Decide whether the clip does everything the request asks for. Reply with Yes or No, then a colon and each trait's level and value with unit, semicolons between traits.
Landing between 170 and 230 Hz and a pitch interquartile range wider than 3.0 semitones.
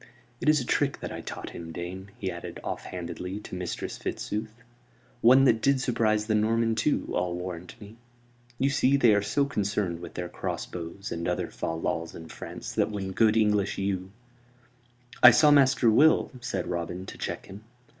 No: low, 105 Hz; average, 5.0 semitones